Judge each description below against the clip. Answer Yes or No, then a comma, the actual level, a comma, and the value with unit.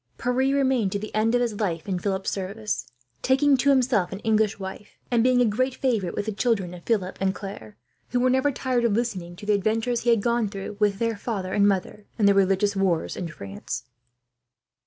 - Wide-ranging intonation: No, average, 3.9 semitones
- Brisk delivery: Yes, fast, 215 wpm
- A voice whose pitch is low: No, high, 210 Hz